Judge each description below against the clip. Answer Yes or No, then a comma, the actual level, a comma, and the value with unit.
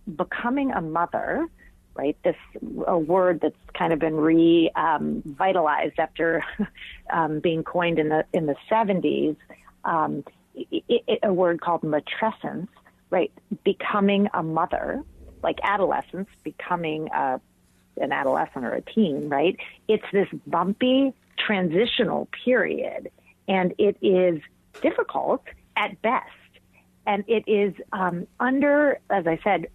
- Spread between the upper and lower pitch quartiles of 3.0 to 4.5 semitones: No, average, 5.1 semitones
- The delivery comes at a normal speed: No, slow, 125 wpm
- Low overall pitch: No, high, 190 Hz